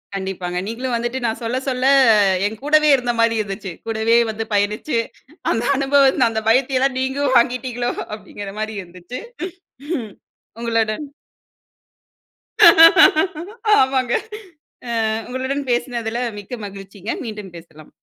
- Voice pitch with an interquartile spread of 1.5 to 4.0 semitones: Yes, average, 3.7 semitones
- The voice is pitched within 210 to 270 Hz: Yes, high, 230 Hz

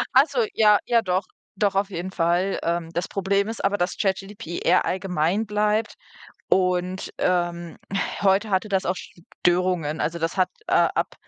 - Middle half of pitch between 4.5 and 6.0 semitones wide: No, narrow, 2.6 semitones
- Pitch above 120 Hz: Yes, high, 190 Hz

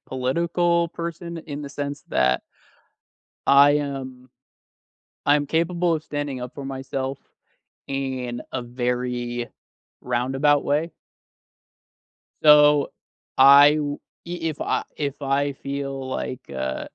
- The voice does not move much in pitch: Yes, narrow, 2.3 semitones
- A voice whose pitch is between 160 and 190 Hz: No, medium, 140 Hz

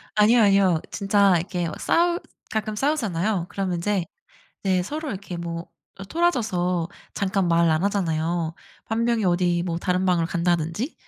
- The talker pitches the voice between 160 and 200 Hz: Yes, medium, 185 Hz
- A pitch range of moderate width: Yes, average, 3.5 semitones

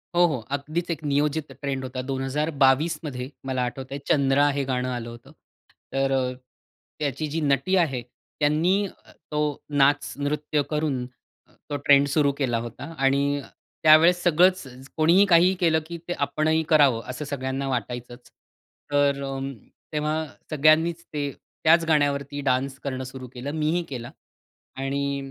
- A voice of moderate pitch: Yes, medium, 145 Hz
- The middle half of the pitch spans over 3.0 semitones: No, narrow, 2.6 semitones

